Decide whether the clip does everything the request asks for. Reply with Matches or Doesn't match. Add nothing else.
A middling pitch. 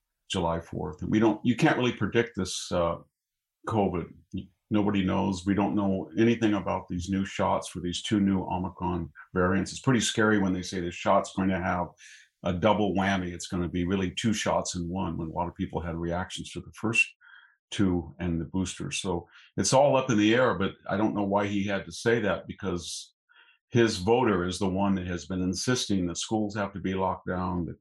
Doesn't match